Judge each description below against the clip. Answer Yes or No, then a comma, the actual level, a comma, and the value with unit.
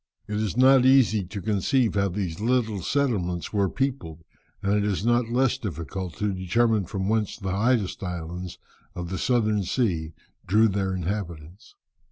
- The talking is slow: No, average, 160 wpm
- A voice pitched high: No, low, 100 Hz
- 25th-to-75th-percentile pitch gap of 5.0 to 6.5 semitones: No, average, 4.2 semitones